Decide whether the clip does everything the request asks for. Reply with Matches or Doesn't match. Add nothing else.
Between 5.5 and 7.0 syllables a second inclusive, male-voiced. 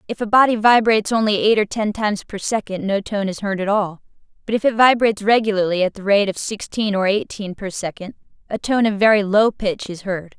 Doesn't match